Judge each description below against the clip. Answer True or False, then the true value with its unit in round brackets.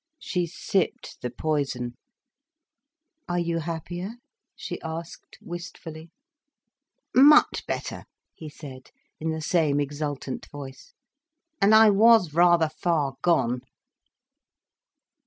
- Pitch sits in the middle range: True (160 Hz)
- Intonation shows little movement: False (3.3 semitones)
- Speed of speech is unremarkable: False (100 wpm)